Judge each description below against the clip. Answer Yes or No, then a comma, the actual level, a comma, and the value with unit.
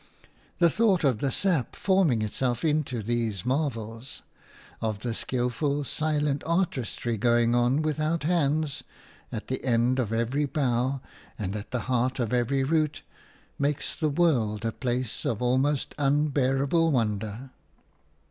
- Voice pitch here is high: No, low, 130 Hz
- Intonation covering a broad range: No, average, 4.0 semitones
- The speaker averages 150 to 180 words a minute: No, slow, 135 wpm